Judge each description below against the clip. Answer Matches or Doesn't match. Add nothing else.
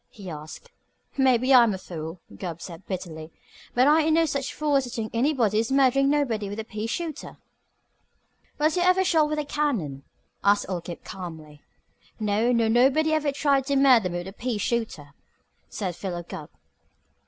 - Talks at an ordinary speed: Matches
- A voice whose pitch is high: Matches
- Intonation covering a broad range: Matches